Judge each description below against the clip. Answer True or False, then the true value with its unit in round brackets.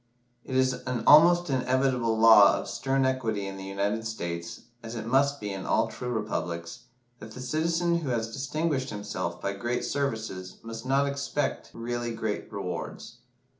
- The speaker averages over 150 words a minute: True (165 wpm)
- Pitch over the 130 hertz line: False (115 Hz)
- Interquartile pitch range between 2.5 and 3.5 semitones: False (4.5 semitones)